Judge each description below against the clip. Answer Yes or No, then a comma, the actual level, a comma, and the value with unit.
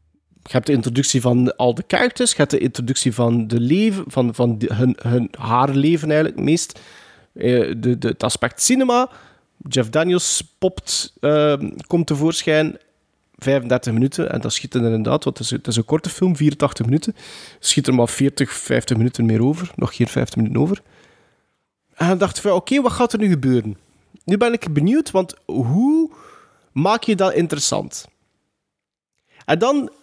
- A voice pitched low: No, medium, 145 Hz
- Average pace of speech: Yes, average, 180 wpm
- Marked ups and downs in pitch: Yes, wide, 6.9 semitones